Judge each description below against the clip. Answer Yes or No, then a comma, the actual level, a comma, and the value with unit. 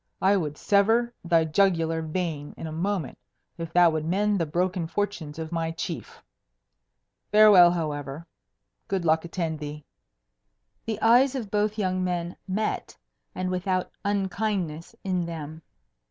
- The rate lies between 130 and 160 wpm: Yes, average, 140 wpm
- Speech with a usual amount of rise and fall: Yes, average, 3.7 semitones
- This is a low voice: No, medium, 175 Hz